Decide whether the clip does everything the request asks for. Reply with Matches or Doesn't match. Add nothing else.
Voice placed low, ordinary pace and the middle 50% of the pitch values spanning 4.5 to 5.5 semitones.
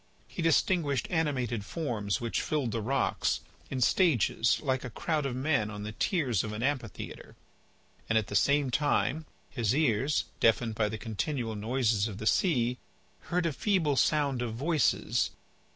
Matches